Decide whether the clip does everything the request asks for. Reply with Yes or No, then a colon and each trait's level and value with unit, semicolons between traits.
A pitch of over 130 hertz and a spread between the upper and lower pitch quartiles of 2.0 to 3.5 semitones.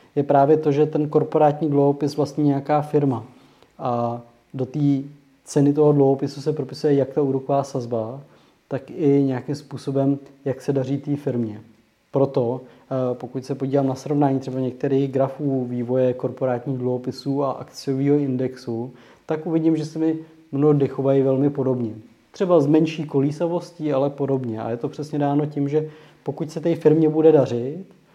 Yes: medium, 140 Hz; narrow, 2.4 semitones